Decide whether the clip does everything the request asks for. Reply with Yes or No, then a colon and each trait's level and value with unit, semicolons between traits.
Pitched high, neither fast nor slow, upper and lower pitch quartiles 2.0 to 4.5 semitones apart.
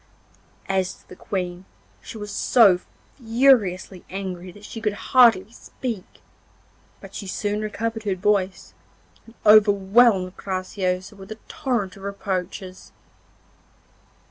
No: high, 200 Hz; slow, 115 wpm; average, 2.9 semitones